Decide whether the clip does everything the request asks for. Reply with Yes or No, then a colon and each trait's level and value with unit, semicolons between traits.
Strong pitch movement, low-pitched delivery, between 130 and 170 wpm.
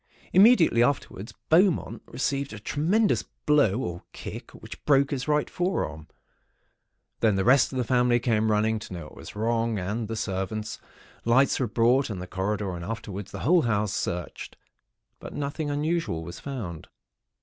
Yes: wide, 5.8 semitones; low, 115 Hz; average, 160 wpm